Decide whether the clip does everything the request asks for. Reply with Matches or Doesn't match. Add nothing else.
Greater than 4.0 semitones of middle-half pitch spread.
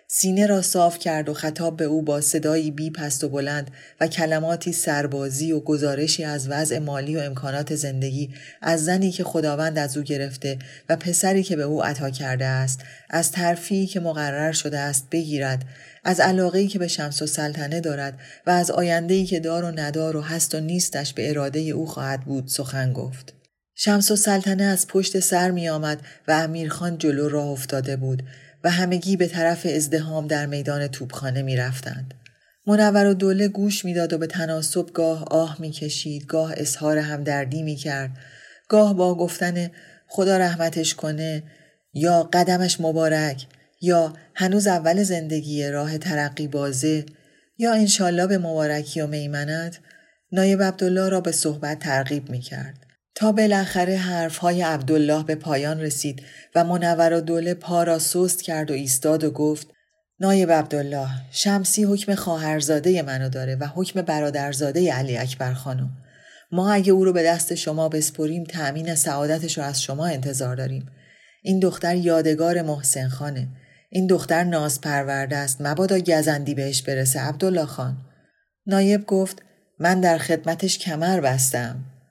Doesn't match